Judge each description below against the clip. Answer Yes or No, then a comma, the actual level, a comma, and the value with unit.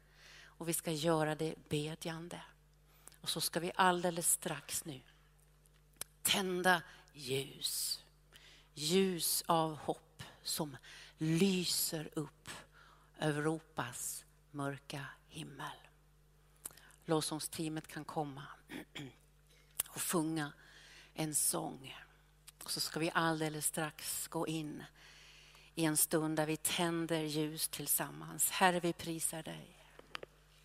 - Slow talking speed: Yes, slow, 100 wpm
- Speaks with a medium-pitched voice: Yes, medium, 155 Hz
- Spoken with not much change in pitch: Yes, narrow, 1.5 semitones